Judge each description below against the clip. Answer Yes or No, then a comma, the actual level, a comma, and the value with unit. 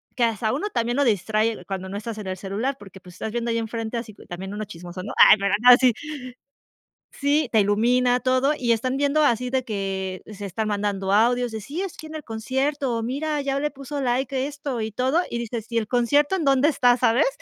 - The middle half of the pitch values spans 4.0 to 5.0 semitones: Yes, average, 4.3 semitones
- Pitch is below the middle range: No, high, 235 Hz